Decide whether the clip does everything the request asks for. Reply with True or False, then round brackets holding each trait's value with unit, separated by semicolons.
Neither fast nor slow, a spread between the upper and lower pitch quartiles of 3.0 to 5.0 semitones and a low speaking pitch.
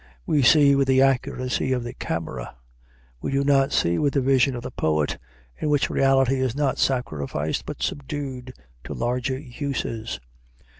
False (160 wpm; 2.4 semitones; 130 Hz)